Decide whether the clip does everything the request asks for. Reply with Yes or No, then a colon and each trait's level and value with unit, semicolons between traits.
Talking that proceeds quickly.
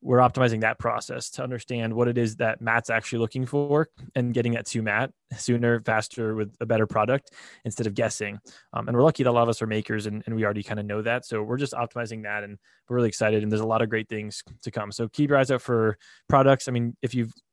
Yes: fast, 260 wpm